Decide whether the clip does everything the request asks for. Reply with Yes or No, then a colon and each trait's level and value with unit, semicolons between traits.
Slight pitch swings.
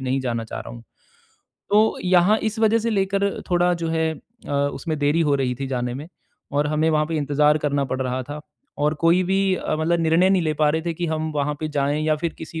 No: average, 3.5 semitones